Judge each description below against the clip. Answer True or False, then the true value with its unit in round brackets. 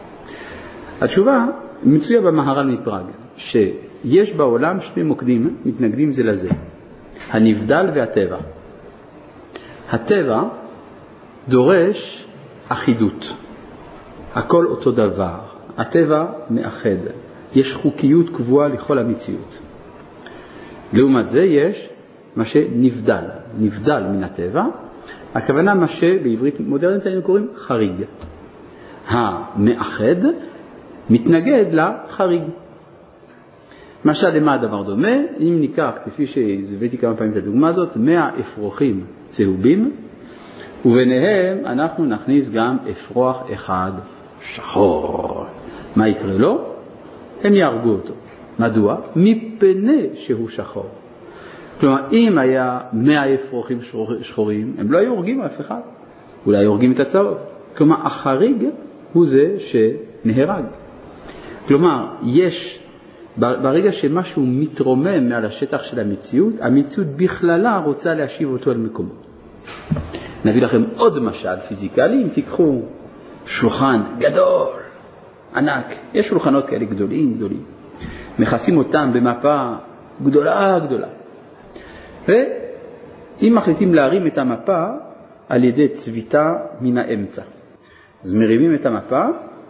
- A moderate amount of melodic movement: False (8.2 semitones)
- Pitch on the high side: False (140 Hz)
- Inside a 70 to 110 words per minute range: True (100 wpm)